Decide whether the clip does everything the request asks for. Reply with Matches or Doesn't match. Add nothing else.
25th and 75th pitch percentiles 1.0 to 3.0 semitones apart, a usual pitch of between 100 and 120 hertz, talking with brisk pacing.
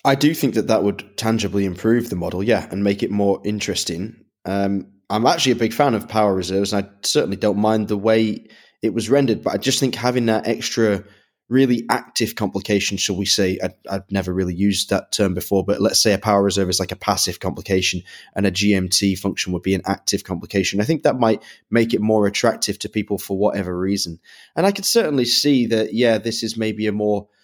Matches